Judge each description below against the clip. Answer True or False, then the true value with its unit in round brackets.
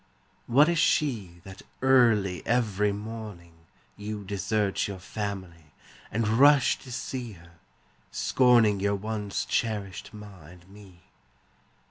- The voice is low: True (105 Hz)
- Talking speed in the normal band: False (115 wpm)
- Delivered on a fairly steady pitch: False (3.3 semitones)